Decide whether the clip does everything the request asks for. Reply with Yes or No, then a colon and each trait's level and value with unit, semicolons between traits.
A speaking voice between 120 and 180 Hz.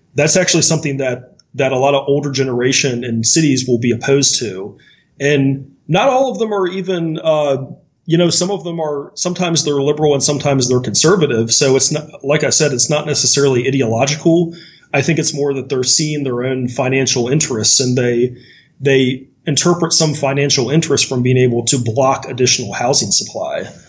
Yes: medium, 140 Hz